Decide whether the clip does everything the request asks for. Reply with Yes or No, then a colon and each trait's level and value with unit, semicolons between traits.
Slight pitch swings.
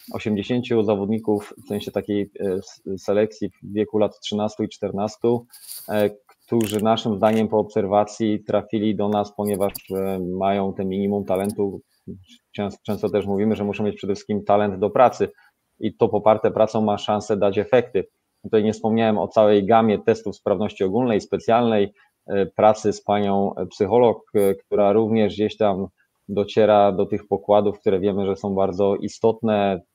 Yes: narrow, 1.2 semitones